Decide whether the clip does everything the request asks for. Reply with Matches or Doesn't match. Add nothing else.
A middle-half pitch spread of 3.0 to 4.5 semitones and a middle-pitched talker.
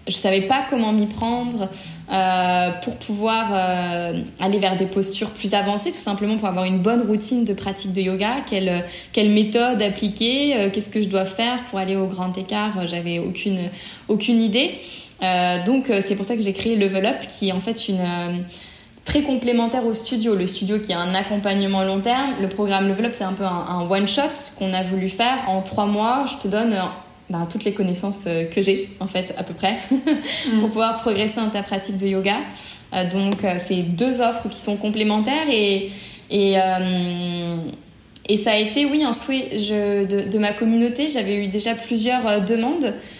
Doesn't match